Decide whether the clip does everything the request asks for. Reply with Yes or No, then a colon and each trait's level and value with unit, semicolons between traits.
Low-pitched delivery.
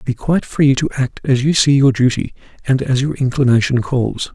Yes: low, 130 Hz